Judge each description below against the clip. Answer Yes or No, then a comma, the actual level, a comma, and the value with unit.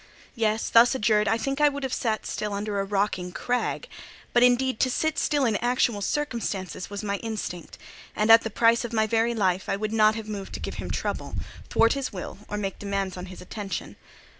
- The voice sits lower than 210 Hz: No, high, 215 Hz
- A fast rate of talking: Yes, fast, 215 wpm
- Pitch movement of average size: Yes, average, 3.1 semitones